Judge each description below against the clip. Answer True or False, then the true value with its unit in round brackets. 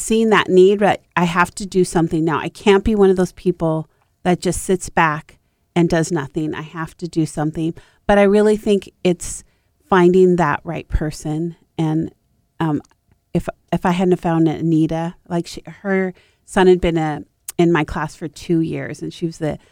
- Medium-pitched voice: True (170 Hz)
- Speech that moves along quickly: False (195 wpm)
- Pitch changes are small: True (2.3 semitones)